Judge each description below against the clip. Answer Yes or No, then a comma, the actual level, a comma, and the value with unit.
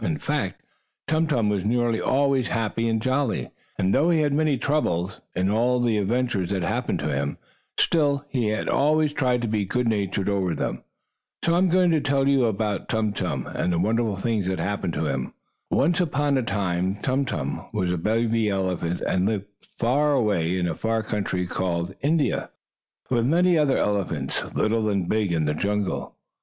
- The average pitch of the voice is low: Yes, low, 110 Hz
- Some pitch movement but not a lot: No, wide, 6.2 semitones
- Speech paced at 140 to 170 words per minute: No, average, 190 wpm